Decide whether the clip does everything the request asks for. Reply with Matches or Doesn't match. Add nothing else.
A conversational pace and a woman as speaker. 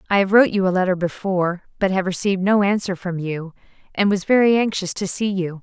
Doesn't match